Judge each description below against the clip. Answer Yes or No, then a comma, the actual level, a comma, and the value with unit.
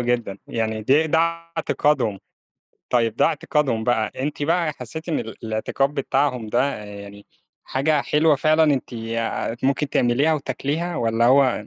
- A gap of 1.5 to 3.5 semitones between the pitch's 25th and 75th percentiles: No, average, 4.8 semitones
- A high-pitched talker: No, low, 130 Hz